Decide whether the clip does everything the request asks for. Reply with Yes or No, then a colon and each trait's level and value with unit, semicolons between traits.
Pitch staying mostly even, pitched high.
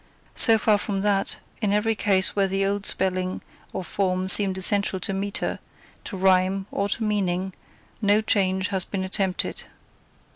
Yes: narrow, 1.4 semitones; high, 195 Hz